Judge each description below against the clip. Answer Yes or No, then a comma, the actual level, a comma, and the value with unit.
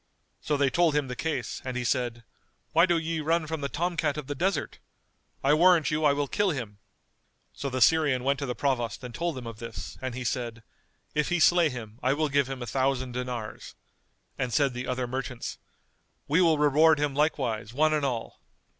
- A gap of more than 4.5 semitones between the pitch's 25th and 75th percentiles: No, average, 3.7 semitones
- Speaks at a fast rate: Yes, fast, 210 wpm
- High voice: No, medium, 140 Hz